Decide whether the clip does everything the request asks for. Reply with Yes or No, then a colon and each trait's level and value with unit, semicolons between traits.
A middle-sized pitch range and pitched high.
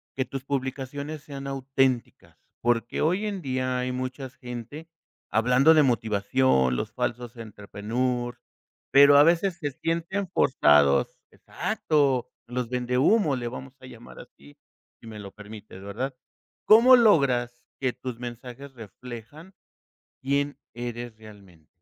No: average, 3.3 semitones; low, 125 Hz